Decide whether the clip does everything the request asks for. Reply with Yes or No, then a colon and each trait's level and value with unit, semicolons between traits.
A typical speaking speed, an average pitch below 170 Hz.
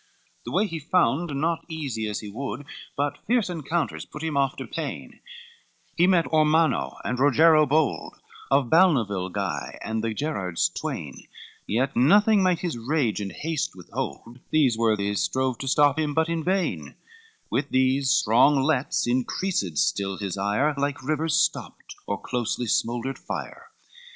Yes: average, 155 wpm; medium, 140 Hz